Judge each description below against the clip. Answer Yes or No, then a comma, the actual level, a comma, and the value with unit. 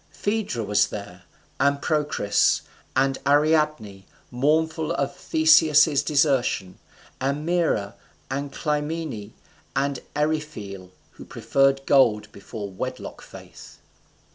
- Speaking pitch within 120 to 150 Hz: Yes, medium, 140 Hz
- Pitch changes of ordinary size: No, wide, 6.2 semitones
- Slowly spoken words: Yes, slow, 95 wpm